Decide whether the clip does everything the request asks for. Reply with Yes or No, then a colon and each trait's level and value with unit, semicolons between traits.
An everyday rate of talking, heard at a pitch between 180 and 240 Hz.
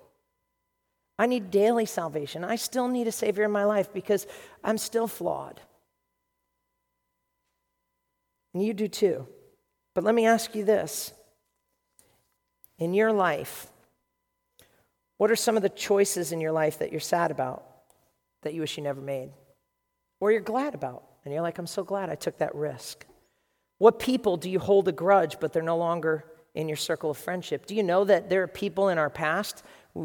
Yes: average, 175 wpm; high, 190 Hz